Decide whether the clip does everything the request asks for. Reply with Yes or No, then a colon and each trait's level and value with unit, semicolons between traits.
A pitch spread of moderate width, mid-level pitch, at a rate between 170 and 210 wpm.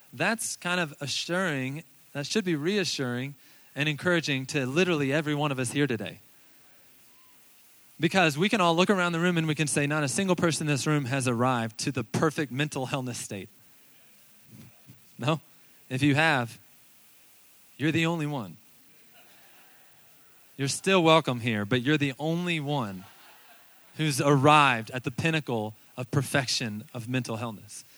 No: average, 4.0 semitones; medium, 145 Hz; average, 155 wpm